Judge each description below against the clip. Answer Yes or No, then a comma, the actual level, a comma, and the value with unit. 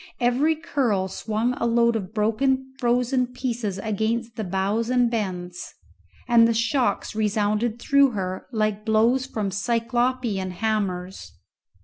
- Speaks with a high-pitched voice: Yes, high, 225 Hz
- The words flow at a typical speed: No, slow, 125 wpm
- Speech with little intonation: No, average, 3.0 semitones